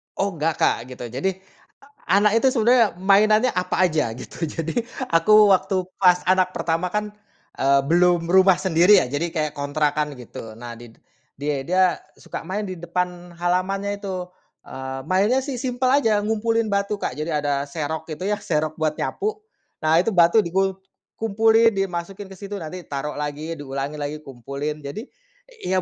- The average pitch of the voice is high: No, medium, 180 Hz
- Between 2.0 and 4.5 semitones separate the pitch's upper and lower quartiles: No, average, 5.2 semitones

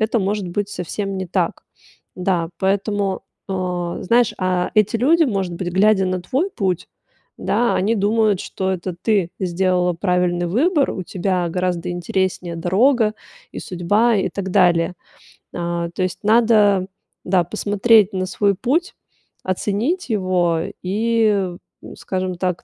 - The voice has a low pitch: No, high, 190 Hz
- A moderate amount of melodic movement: Yes, average, 3.0 semitones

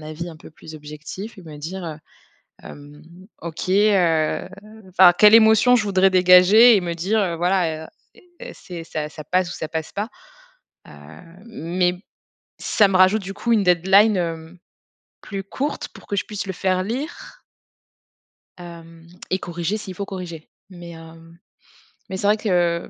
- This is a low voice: No, medium, 180 Hz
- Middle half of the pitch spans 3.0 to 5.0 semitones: Yes, average, 3.4 semitones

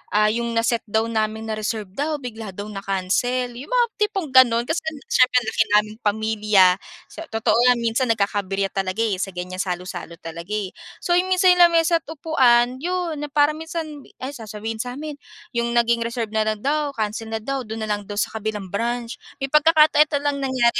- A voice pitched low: No, high, 230 Hz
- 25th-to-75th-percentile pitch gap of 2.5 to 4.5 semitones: No, average, 5.2 semitones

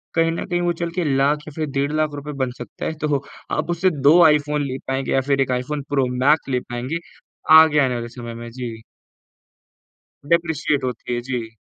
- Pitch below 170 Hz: Yes, medium, 140 Hz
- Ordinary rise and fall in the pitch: Yes, average, 3.6 semitones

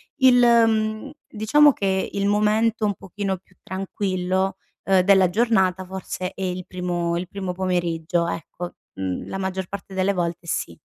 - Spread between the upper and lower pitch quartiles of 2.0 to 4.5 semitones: Yes, narrow, 2.5 semitones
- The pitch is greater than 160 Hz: Yes, high, 190 Hz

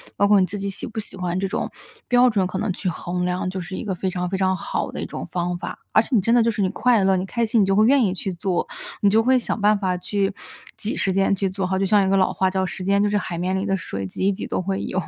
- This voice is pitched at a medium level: No, high, 195 Hz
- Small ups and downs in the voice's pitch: Yes, narrow, 2.1 semitones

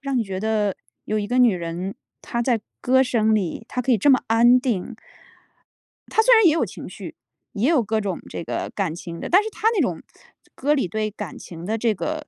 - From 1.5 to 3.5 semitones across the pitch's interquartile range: No, average, 4.6 semitones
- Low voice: No, high, 225 Hz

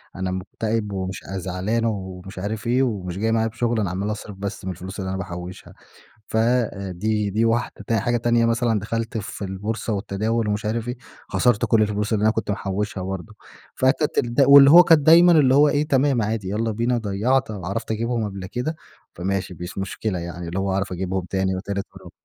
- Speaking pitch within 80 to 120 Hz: Yes, low, 105 Hz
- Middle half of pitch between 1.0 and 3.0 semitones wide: No, average, 3.5 semitones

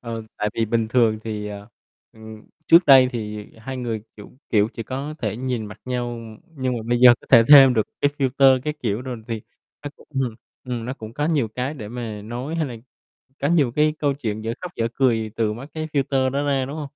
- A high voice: No, low, 120 Hz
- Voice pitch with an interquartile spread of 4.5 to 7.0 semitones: No, average, 3.6 semitones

